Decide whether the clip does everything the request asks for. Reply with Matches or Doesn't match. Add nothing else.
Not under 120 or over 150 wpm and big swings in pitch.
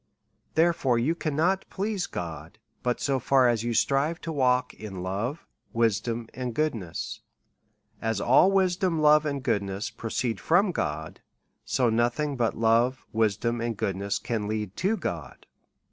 Matches